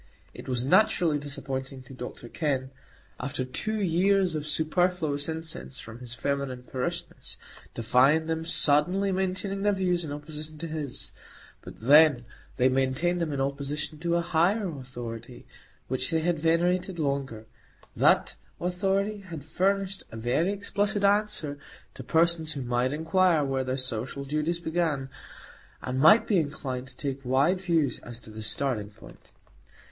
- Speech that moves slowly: No, average, 150 wpm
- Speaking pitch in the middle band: Yes, medium, 150 Hz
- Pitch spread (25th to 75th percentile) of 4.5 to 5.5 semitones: Yes, average, 5.0 semitones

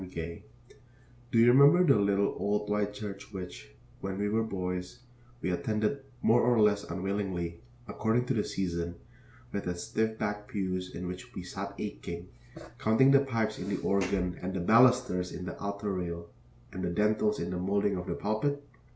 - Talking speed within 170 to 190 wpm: Yes, average, 175 wpm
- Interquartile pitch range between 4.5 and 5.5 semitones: No, average, 3.1 semitones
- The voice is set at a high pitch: No, low, 100 Hz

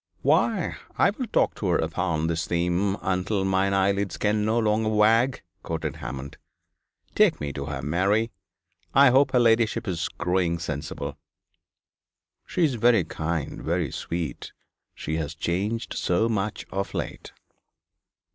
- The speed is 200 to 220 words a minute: No, average, 140 wpm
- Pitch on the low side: Yes, very low, 95 Hz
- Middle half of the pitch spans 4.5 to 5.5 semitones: Yes, average, 4.9 semitones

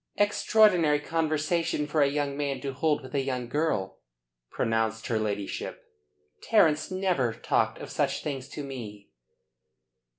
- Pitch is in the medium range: Yes, medium, 145 Hz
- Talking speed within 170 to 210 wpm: No, slow, 135 wpm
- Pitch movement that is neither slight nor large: Yes, average, 4.3 semitones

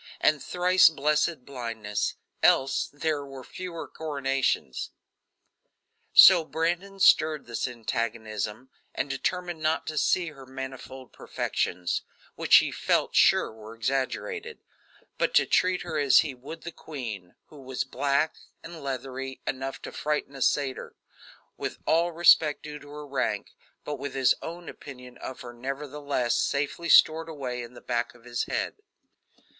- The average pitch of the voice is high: No, medium, 140 Hz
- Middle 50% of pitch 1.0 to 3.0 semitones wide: No, average, 4.0 semitones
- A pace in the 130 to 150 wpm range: Yes, average, 145 wpm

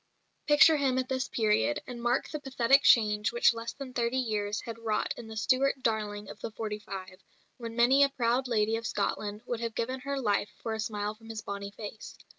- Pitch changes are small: No, average, 3.4 semitones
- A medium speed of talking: No, fast, 215 wpm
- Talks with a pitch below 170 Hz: No, high, 230 Hz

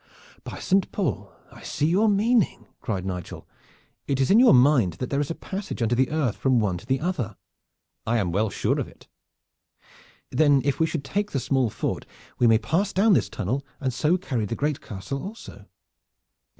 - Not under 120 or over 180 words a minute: No, average, 195 wpm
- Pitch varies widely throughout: Yes, wide, 7.3 semitones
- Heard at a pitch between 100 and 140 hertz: Yes, low, 135 Hz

